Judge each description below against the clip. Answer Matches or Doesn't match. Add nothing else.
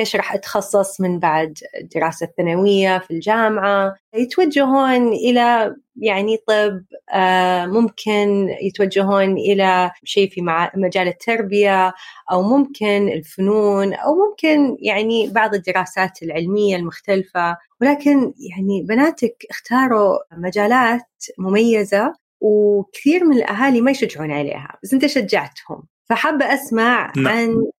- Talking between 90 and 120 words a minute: Matches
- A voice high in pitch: Matches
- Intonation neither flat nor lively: Matches